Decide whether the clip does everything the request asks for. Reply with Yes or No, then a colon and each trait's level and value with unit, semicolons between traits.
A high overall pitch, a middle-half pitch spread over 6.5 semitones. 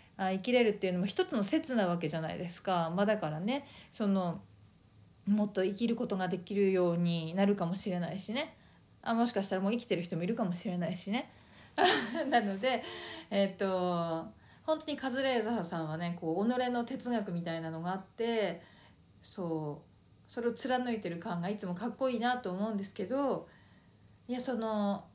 No: high, 200 Hz; average, 5.3 semitones